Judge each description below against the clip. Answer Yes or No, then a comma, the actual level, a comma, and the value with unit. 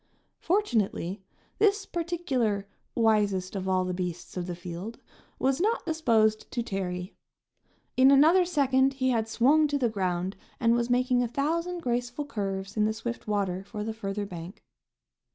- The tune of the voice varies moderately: No, wide, 5.9 semitones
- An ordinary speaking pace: Yes, average, 155 wpm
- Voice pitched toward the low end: No, high, 225 Hz